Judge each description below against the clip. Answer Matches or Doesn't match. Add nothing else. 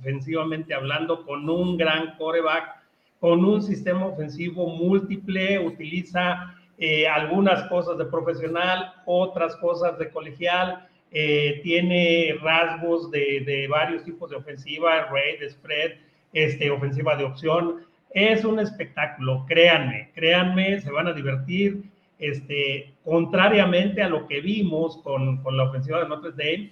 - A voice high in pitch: Doesn't match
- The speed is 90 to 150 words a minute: Matches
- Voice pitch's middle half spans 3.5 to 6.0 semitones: Doesn't match